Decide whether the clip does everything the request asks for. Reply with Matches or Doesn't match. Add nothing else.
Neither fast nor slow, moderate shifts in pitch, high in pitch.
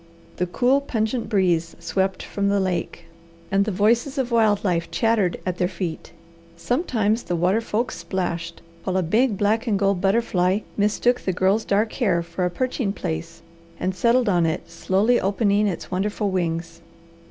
Matches